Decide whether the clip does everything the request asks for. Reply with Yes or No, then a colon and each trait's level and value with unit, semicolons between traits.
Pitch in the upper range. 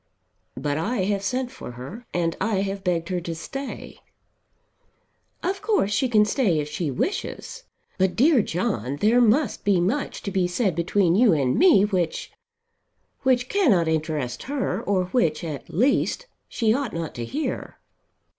Yes: high, 195 Hz